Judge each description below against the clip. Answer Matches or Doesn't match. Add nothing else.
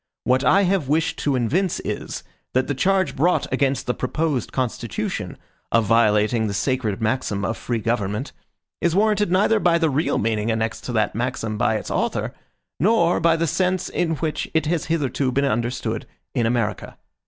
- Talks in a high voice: Doesn't match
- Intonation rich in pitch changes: Matches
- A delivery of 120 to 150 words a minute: Doesn't match